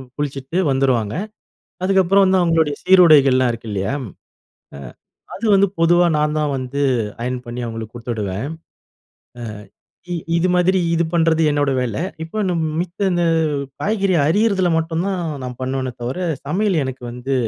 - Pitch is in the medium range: Yes, medium, 150 Hz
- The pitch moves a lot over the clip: Yes, wide, 5.9 semitones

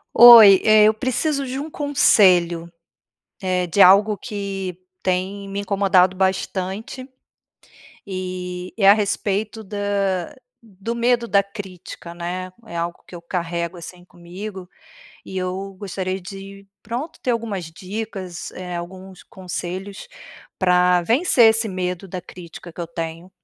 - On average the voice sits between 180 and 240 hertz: Yes, high, 190 Hz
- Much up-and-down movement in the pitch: No, narrow, 2.6 semitones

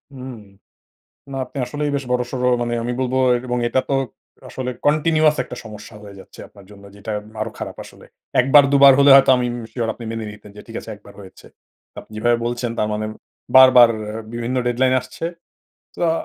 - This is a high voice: No, low, 120 Hz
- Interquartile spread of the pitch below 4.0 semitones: Yes, average, 2.9 semitones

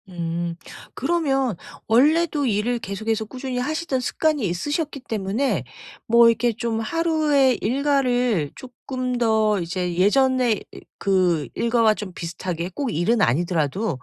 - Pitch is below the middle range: No, high, 230 Hz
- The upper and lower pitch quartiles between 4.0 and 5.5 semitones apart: No, wide, 5.9 semitones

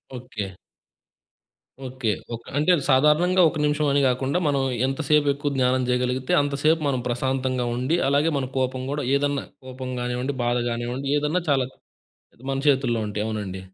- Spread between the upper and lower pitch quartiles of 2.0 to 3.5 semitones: Yes, narrow, 2.5 semitones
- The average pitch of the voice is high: No, low, 130 Hz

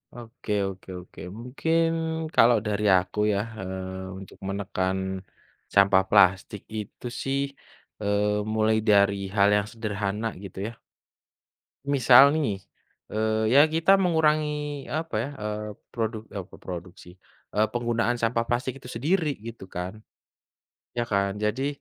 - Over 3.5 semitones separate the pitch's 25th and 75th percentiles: Yes, average, 4.4 semitones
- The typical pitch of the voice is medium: No, low, 110 Hz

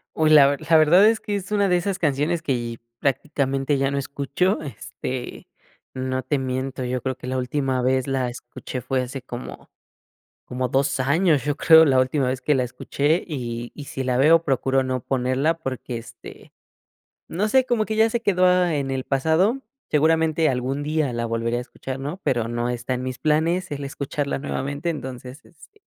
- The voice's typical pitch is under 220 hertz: Yes, low, 135 Hz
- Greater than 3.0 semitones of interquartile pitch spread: Yes, average, 3.8 semitones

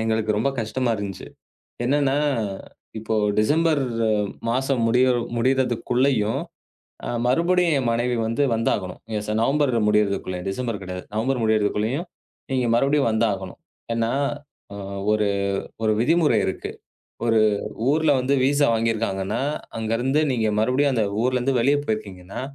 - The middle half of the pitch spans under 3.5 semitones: No, average, 3.9 semitones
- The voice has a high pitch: No, low, 115 Hz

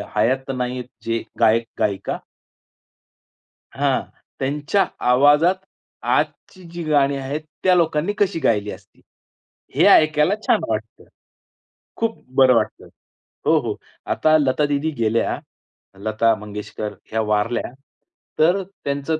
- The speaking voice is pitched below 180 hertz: Yes, low, 135 Hz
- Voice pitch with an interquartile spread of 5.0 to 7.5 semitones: Yes, wide, 5.5 semitones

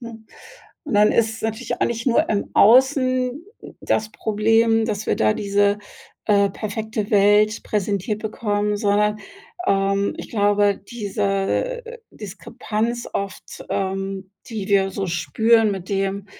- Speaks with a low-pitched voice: No, high, 210 Hz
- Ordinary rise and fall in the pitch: No, narrow, 2.0 semitones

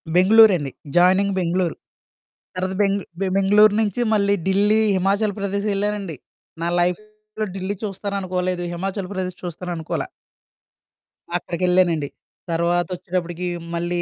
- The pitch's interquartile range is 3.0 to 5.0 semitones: No, narrow, 2.4 semitones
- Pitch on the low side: No, medium, 185 Hz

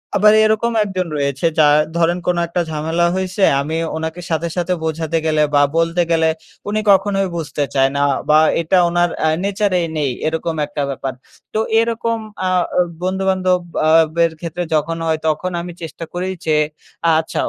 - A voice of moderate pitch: Yes, medium, 170 Hz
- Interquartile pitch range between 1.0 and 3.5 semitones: Yes, average, 2.9 semitones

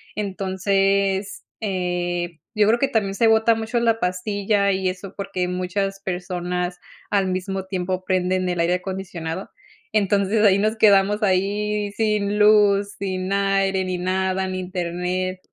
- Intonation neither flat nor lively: No, narrow, 1.9 semitones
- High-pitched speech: Yes, high, 195 Hz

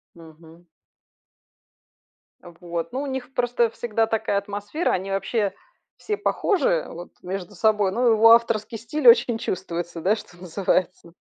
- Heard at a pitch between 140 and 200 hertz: No, high, 210 Hz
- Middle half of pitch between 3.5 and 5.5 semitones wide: Yes, average, 4.7 semitones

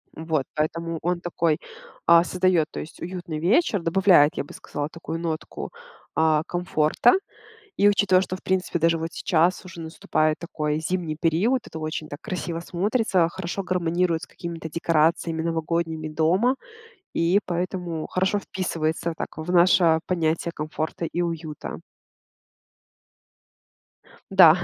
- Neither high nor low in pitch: Yes, medium, 170 Hz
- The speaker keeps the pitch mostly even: Yes, narrow, 2.3 semitones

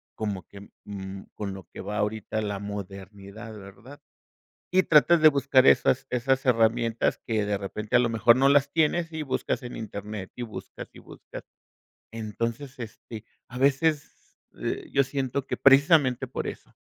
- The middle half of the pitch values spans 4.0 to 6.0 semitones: Yes, average, 4.8 semitones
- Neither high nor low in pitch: No, low, 115 Hz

